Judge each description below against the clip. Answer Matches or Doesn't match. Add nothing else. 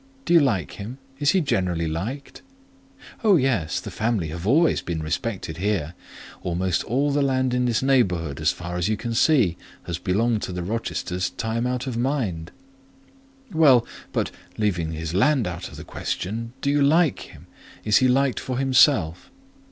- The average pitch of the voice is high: Doesn't match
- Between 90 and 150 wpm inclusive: Doesn't match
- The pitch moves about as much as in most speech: Doesn't match